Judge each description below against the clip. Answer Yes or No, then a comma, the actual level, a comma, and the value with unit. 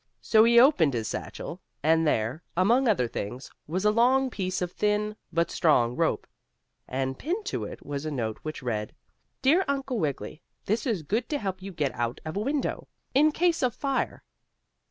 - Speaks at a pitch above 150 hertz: Yes, high, 190 Hz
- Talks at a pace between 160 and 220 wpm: Yes, average, 185 wpm